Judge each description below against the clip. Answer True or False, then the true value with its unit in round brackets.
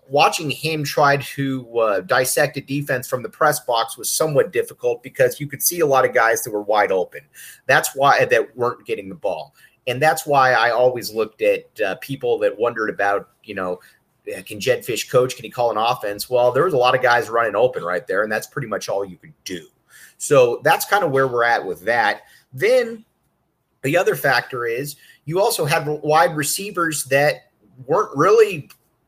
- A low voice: False (170 Hz)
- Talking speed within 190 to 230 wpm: True (200 wpm)